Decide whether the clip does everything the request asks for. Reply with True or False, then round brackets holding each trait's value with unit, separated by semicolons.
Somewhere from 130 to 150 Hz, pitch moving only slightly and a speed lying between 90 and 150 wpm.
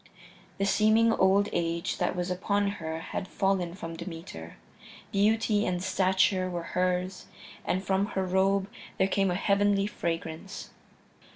False (190 Hz; 2.0 semitones; 135 wpm)